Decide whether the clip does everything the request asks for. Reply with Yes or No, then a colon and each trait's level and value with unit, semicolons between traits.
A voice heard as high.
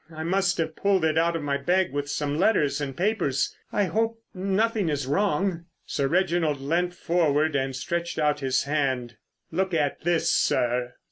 No: medium, 160 Hz